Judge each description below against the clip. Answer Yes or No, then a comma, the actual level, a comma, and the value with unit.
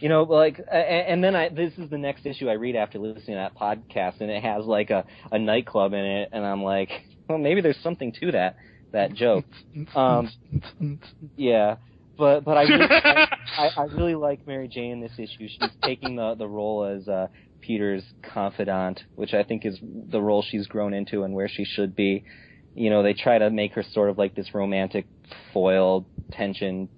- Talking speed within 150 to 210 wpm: Yes, average, 200 wpm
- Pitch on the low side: Yes, low, 110 Hz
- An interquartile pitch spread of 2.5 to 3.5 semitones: No, wide, 6.1 semitones